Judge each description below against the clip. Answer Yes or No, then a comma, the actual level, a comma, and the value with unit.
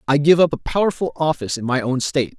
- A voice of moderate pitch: Yes, medium, 145 Hz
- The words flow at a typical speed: No, fast, 250 wpm